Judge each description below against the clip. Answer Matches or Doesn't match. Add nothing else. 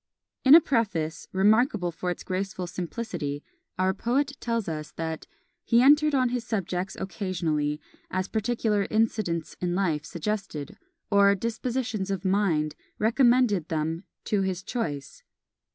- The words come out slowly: Matches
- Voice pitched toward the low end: Doesn't match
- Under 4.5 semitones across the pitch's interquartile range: Doesn't match